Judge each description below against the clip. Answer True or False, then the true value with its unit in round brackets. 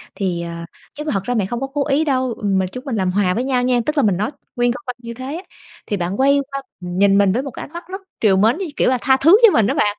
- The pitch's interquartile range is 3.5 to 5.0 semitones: False (5.6 semitones)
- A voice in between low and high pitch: False (240 Hz)